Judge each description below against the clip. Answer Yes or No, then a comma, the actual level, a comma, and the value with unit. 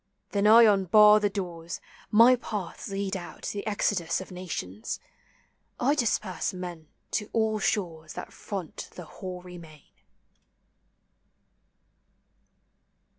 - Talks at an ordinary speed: No, slow, 110 wpm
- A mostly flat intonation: No, average, 3.3 semitones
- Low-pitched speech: No, high, 195 Hz